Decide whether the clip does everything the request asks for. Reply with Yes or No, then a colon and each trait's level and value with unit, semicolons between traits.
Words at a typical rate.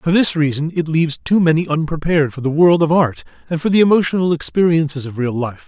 No: fast, 220 wpm